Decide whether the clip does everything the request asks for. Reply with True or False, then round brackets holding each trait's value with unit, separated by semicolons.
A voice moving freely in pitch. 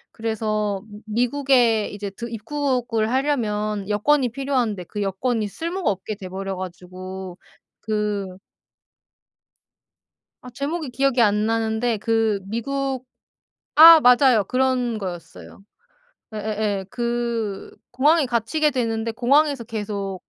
False (3.7 semitones)